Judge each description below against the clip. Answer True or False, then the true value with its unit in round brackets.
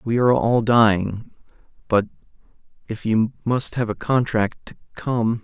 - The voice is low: True (115 Hz)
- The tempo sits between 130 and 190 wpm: True (145 wpm)